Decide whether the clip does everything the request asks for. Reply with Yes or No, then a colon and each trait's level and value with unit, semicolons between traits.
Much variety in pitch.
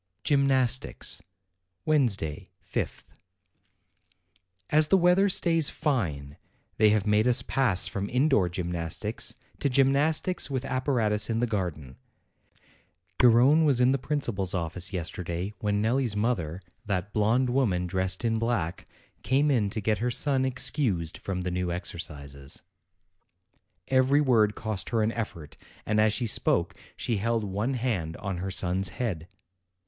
Yes: wide, 6.1 semitones